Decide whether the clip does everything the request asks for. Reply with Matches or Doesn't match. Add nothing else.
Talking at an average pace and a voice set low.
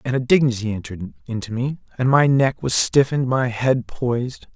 Matches